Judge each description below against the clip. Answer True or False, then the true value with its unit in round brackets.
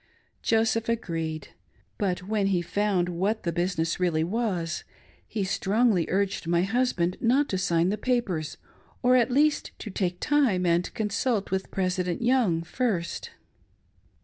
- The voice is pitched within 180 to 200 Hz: True (190 Hz)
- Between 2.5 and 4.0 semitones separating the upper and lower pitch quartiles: False (4.6 semitones)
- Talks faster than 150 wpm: False (140 wpm)